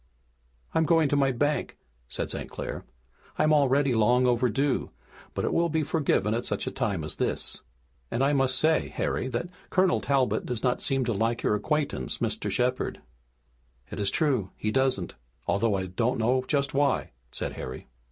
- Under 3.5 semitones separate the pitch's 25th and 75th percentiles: No, average, 4.0 semitones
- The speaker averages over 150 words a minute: Yes, average, 175 wpm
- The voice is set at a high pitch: No, low, 130 Hz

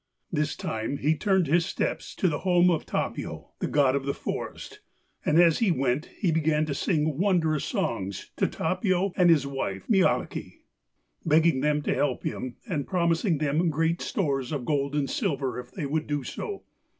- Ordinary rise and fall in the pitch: Yes, average, 3.8 semitones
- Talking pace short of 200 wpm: Yes, average, 180 wpm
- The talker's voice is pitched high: No, medium, 155 Hz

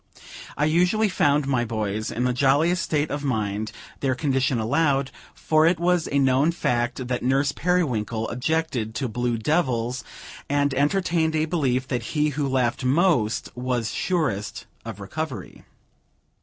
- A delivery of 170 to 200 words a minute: No, average, 145 wpm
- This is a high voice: No, low, 135 Hz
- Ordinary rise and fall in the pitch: Yes, average, 4.5 semitones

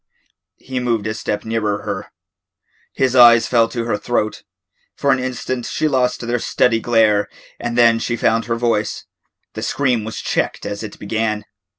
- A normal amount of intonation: No, narrow, 2.2 semitones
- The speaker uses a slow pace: No, average, 170 wpm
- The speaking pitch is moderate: No, low, 115 Hz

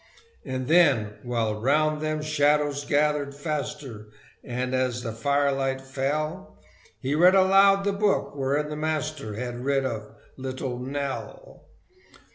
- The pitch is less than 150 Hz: Yes, medium, 140 Hz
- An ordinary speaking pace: No, slow, 125 wpm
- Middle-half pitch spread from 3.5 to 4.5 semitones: No, average, 3.0 semitones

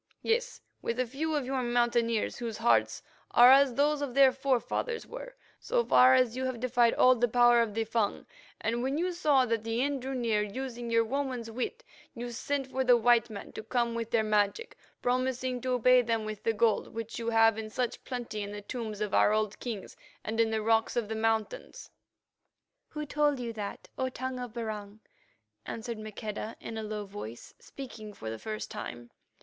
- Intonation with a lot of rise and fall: No, average, 2.8 semitones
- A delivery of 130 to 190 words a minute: No, average, 200 wpm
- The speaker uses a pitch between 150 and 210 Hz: No, high, 235 Hz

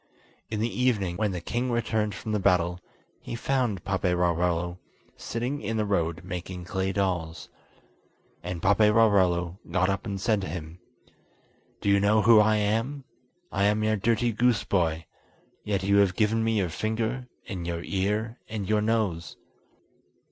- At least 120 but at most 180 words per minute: Yes, average, 155 wpm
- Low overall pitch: Yes, low, 100 Hz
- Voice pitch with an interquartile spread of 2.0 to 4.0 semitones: Yes, average, 3.6 semitones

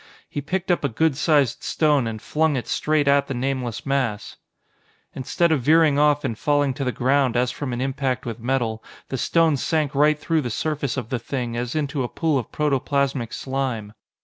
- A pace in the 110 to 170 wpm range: No, average, 200 wpm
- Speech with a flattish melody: No, average, 3.3 semitones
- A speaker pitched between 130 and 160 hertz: Yes, low, 135 Hz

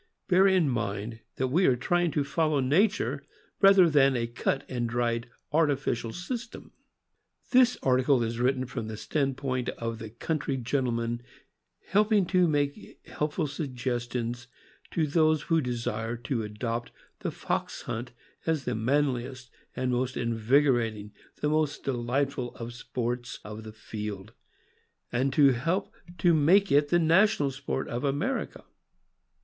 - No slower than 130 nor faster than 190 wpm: Yes, average, 145 wpm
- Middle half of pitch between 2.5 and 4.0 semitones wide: No, average, 4.4 semitones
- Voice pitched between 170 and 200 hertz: No, low, 130 Hz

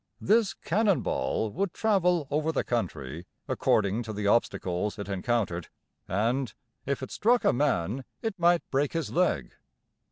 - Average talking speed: Yes, average, 150 wpm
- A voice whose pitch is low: Yes, low, 130 Hz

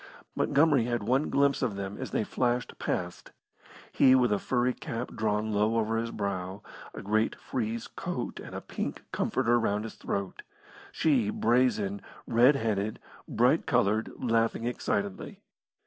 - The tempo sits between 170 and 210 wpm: No, average, 145 wpm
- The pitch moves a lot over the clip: No, average, 3.0 semitones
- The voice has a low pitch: Yes, low, 115 Hz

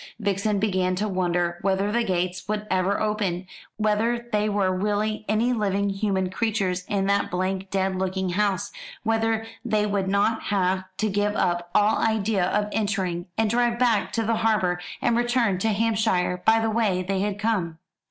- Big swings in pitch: No, average, 2.7 semitones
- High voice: Yes, high, 205 Hz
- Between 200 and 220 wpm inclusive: No, average, 170 wpm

